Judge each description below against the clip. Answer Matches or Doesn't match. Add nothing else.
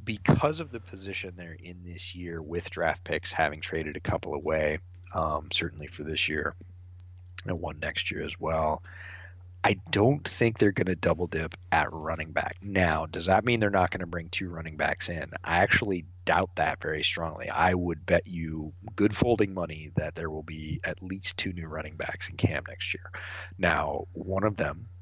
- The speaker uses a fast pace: Doesn't match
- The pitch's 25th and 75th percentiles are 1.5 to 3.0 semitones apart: Matches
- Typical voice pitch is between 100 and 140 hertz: Doesn't match